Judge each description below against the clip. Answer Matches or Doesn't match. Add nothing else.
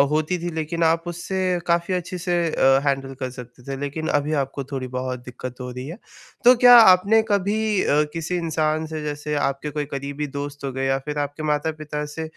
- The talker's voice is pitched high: Doesn't match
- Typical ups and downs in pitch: Matches